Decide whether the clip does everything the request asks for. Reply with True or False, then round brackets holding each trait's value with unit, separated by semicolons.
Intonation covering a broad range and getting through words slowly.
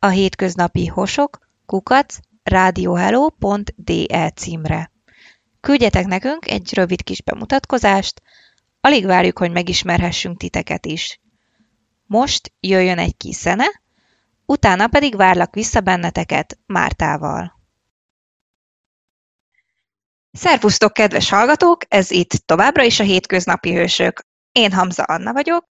True (6.6 semitones; 100 wpm)